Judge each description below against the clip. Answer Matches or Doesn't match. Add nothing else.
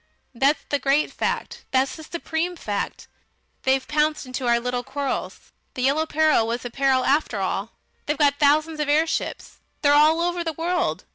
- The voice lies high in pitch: Matches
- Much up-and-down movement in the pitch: Doesn't match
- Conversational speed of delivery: Matches